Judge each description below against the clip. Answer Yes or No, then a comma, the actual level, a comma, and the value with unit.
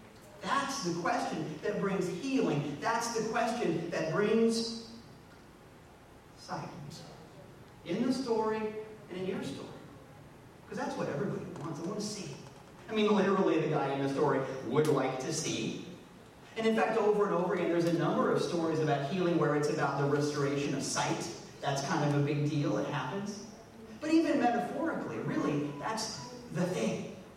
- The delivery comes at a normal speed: Yes, average, 165 wpm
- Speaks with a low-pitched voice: No, medium, 180 Hz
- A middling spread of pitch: No, wide, 6.3 semitones